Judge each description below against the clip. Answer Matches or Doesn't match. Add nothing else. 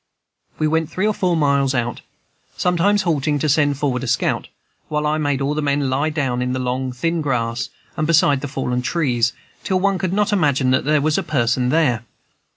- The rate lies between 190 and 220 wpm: Matches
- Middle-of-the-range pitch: Matches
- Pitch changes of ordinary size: Matches